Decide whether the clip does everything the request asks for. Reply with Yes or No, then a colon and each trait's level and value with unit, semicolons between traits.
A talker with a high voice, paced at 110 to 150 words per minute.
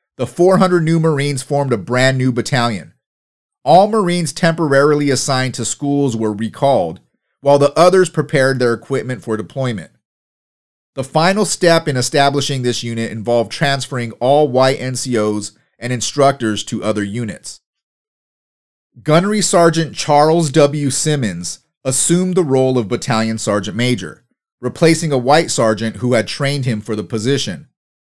No: low, 135 Hz; average, 140 wpm